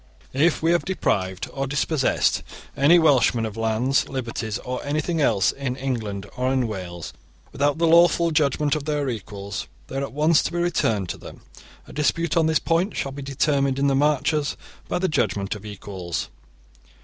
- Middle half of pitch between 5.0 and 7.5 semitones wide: Yes, wide, 5.4 semitones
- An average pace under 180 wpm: No, average, 185 wpm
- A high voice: No, low, 135 Hz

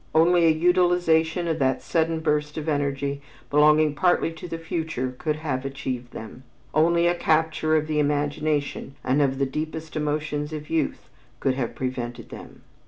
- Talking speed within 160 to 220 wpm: Yes, average, 165 wpm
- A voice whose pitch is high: No, medium, 155 Hz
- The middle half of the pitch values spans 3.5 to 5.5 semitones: No, narrow, 2.4 semitones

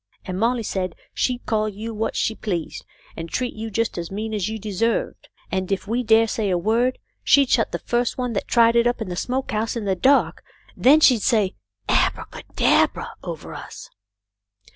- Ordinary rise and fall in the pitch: Yes, average, 3.3 semitones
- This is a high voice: Yes, high, 220 Hz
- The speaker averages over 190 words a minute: Yes, fast, 205 wpm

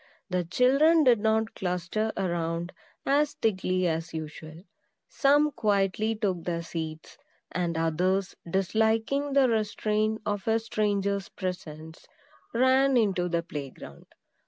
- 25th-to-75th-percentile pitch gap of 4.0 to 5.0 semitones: Yes, average, 4.6 semitones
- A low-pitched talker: No, high, 195 Hz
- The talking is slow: Yes, slow, 120 wpm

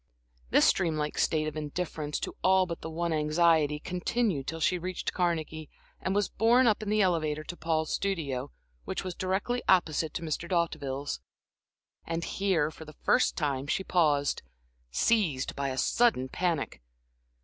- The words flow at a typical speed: Yes, average, 160 wpm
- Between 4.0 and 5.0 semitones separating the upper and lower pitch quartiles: No, average, 3.6 semitones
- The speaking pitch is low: No, medium, 165 Hz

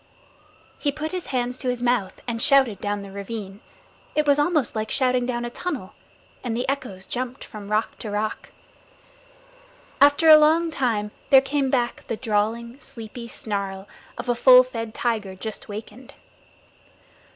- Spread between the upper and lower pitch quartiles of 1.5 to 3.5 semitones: No, average, 4.0 semitones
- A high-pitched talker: Yes, high, 240 Hz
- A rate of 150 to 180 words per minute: Yes, average, 160 wpm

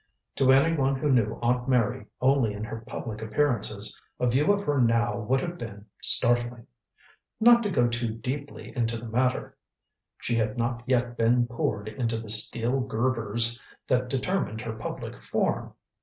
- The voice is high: No, low, 120 Hz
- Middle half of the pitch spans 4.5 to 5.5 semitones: No, narrow, 2.5 semitones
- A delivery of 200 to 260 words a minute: No, average, 165 wpm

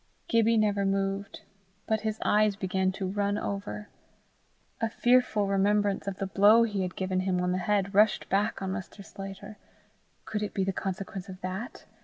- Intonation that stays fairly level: Yes, narrow, 1.7 semitones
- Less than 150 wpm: No, average, 175 wpm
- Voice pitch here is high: Yes, high, 200 Hz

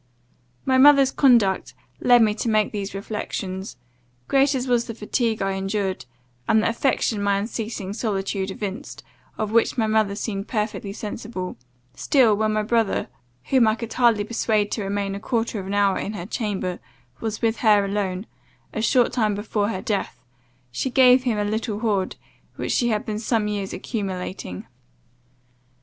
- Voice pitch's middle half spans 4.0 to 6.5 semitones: No, narrow, 2.6 semitones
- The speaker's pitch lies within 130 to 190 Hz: No, high, 215 Hz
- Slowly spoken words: No, average, 165 wpm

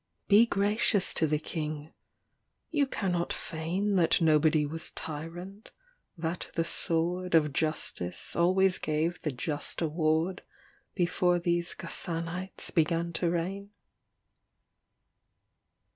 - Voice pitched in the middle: Yes, medium, 170 Hz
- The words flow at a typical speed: No, slow, 110 wpm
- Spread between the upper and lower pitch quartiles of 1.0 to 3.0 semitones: Yes, narrow, 2.4 semitones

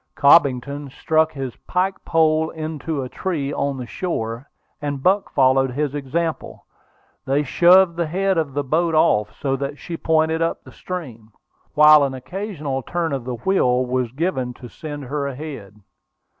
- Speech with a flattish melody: No, average, 3.7 semitones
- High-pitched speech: No, medium, 145 Hz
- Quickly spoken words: No, average, 160 wpm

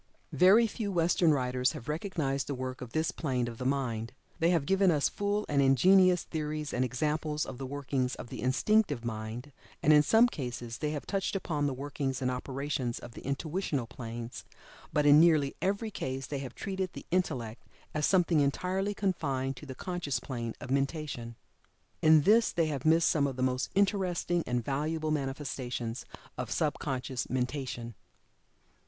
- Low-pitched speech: No, medium, 145 Hz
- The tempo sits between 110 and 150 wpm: No, average, 175 wpm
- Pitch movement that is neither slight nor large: Yes, average, 4.7 semitones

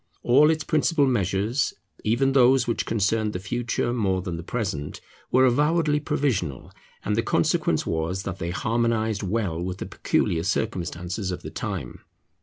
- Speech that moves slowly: No, average, 155 wpm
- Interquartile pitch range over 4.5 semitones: Yes, wide, 5.5 semitones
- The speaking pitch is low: Yes, low, 110 Hz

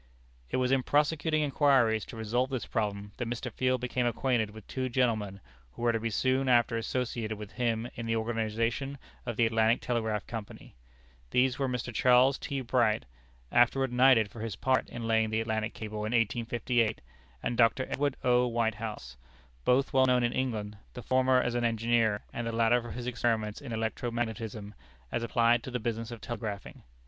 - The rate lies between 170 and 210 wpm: Yes, average, 185 wpm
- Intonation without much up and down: Yes, narrow, 2.1 semitones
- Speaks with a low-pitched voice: Yes, low, 120 Hz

